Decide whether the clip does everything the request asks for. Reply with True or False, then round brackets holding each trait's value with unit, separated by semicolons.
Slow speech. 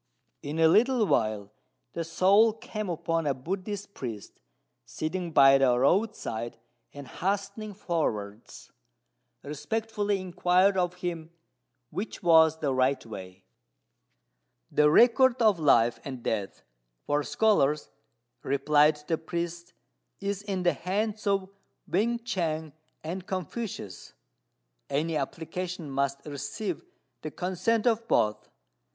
True (115 wpm)